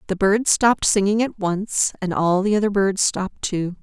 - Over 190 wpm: Yes, fast, 205 wpm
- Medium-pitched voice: No, high, 200 Hz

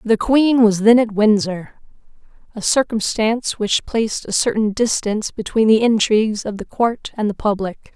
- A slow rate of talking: No, average, 160 wpm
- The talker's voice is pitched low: No, high, 220 Hz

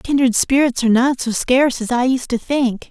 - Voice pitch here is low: No, very high, 250 Hz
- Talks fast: Yes, fast, 225 wpm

